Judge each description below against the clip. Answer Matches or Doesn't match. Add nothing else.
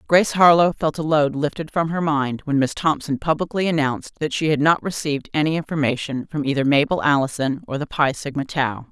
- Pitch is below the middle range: Doesn't match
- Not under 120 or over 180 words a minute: Doesn't match